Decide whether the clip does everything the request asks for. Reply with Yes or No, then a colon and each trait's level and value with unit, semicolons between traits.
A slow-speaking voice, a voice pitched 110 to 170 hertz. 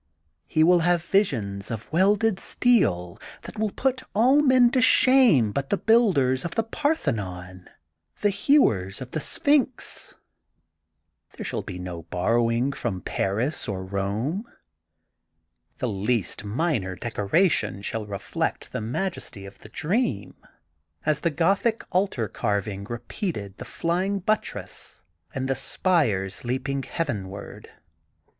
Yes: slow, 125 wpm; low, 135 Hz